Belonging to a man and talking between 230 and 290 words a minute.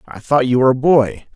Yes: male; fast, 265 wpm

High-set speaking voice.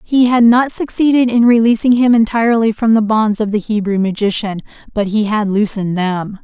Yes: high, 220 Hz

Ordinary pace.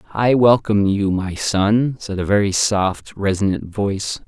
Yes: average, 155 wpm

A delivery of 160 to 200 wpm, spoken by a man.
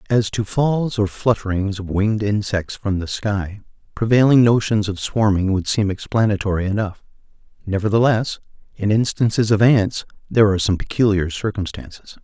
No: average, 140 wpm; male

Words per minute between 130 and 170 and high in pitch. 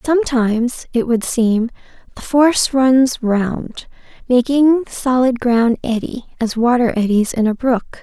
Yes: average, 140 wpm; high, 245 Hz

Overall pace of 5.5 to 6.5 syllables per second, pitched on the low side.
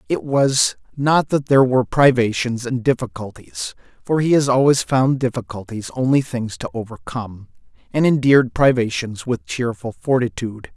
No: 5.0 syllables/s; low, 125 Hz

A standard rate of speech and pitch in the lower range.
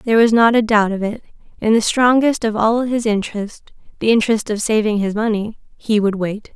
No: average, 190 wpm; high, 220 Hz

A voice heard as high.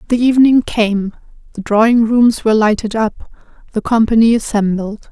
Yes: high, 220 Hz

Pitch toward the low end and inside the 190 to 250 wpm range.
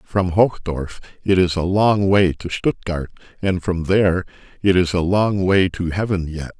No: very low, 90 Hz; average, 180 wpm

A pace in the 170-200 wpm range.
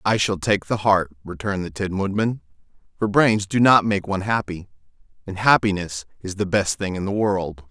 Yes: average, 195 wpm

